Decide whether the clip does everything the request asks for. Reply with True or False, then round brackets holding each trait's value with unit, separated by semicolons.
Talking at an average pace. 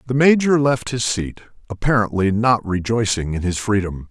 True (160 wpm)